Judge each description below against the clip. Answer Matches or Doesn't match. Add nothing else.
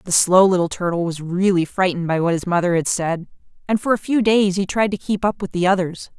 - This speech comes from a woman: Matches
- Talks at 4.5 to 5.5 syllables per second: Doesn't match